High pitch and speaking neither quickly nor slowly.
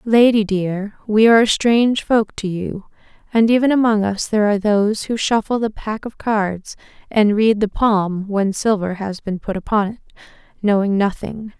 Yes: high, 210 Hz; average, 180 wpm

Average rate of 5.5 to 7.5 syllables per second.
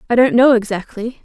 Yes: 5.9 syllables/s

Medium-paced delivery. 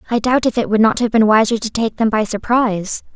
No: fast, 265 wpm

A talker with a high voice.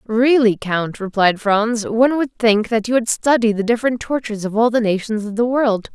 Yes: high, 225 Hz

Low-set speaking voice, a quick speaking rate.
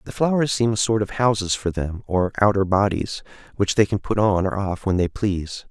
Yes: low, 100 Hz; fast, 230 wpm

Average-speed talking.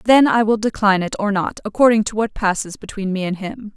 No: fast, 240 wpm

